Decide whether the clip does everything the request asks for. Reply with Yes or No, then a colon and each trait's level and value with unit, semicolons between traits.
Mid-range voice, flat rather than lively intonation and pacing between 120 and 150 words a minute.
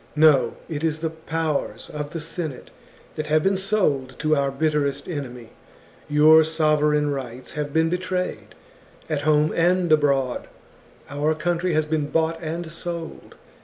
Yes: medium, 155 Hz; narrow, 2.0 semitones; average, 145 wpm